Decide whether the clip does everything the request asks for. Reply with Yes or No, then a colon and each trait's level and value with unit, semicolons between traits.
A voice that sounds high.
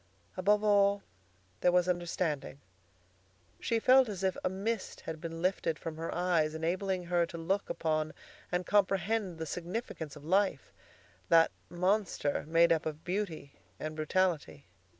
No: medium, 175 Hz